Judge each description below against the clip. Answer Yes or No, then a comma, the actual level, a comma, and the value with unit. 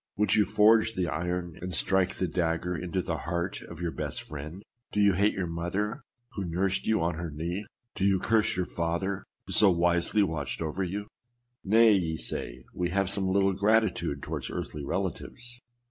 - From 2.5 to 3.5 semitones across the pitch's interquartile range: Yes, average, 3.0 semitones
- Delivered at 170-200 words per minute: Yes, average, 185 wpm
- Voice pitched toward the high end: No, very low, 90 Hz